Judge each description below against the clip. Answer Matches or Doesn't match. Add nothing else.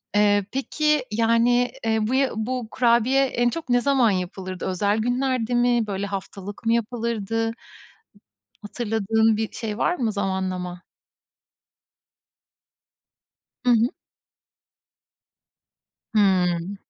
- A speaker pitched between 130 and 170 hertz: Doesn't match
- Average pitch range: Matches